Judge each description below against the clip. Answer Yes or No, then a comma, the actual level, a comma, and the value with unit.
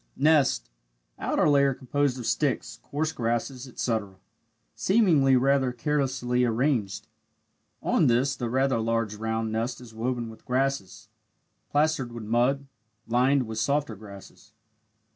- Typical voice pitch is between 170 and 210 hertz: No, low, 125 Hz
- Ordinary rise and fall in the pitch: Yes, average, 3.4 semitones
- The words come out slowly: Yes, slow, 125 wpm